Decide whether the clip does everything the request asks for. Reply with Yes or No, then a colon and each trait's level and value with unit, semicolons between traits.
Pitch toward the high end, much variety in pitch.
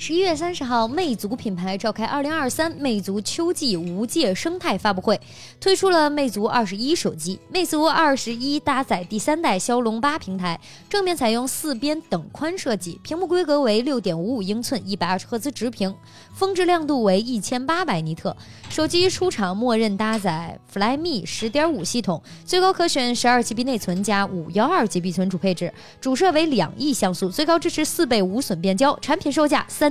Yes: high, 245 Hz; wide, 7.7 semitones